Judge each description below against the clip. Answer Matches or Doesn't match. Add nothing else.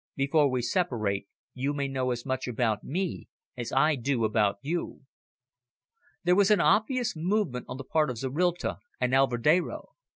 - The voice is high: Doesn't match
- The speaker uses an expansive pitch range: Matches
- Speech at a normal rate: Matches